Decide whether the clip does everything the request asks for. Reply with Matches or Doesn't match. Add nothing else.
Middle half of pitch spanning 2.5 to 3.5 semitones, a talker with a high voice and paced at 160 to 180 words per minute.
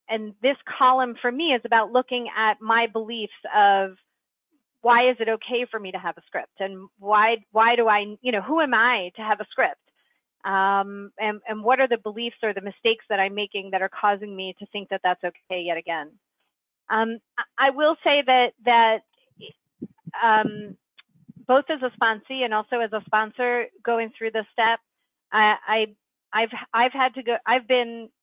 Doesn't match